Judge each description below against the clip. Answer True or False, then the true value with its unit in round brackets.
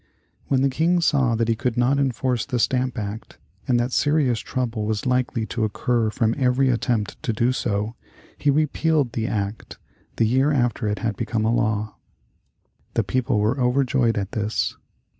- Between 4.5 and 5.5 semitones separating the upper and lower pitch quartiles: False (2.8 semitones)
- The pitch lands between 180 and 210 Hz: False (120 Hz)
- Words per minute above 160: True (175 wpm)